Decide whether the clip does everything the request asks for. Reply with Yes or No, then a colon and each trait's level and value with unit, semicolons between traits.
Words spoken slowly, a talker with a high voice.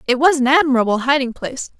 No: average, 200 wpm; very high, 270 Hz